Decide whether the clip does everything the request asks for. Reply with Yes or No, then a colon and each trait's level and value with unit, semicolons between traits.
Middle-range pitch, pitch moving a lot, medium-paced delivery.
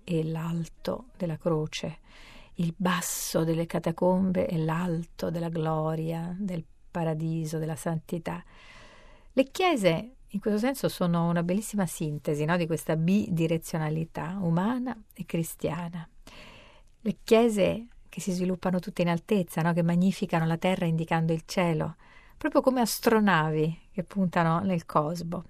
No: medium, 175 Hz; narrow, 2.4 semitones; average, 130 wpm